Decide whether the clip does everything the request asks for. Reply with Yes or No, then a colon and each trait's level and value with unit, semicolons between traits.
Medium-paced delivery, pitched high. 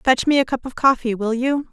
No: fast, 280 wpm; very high, 255 Hz